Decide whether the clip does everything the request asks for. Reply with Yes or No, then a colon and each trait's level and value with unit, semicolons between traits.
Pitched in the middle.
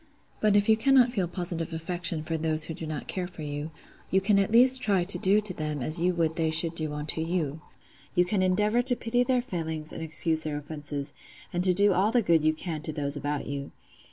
Yes: medium, 170 Hz